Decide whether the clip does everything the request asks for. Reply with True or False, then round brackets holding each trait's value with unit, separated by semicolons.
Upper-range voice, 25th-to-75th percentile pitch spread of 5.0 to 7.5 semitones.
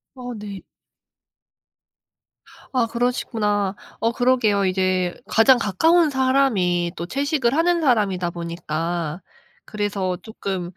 True (210 Hz; 5.5 semitones)